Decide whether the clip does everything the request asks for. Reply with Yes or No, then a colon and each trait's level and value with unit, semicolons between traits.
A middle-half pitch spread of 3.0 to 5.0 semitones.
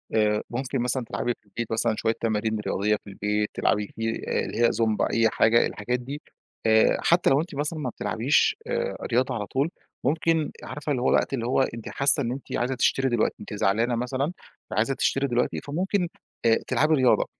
Yes: average, 3.7 semitones